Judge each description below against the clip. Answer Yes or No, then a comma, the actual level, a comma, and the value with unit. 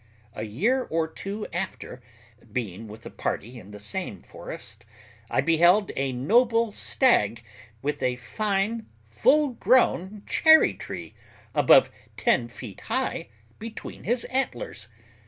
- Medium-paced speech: No, slow, 125 wpm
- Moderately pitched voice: Yes, medium, 170 Hz